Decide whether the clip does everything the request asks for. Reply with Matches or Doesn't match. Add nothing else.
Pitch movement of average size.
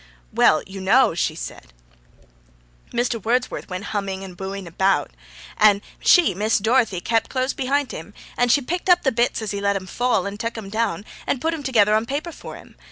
Matches